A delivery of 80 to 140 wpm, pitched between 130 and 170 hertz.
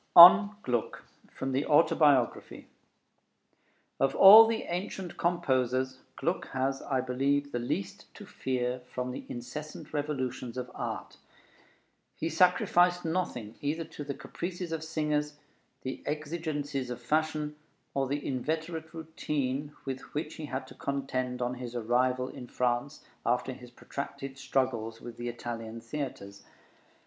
Yes: slow, 135 wpm; low, 135 Hz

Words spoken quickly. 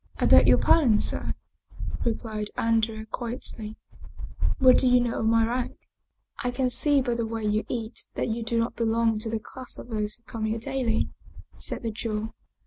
Yes: fast, 215 wpm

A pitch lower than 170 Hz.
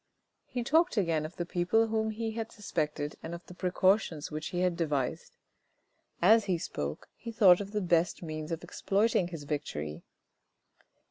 No: medium, 175 Hz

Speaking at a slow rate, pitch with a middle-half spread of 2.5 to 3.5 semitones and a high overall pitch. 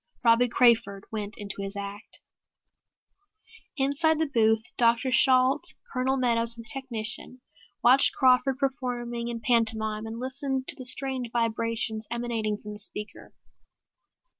Yes: slow, 130 wpm; average, 2.8 semitones; high, 235 Hz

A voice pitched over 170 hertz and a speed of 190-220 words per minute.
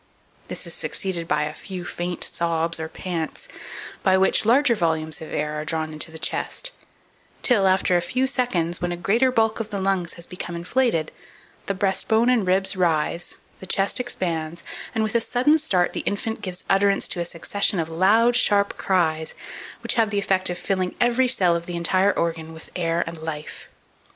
Yes: medium, 185 Hz; average, 195 wpm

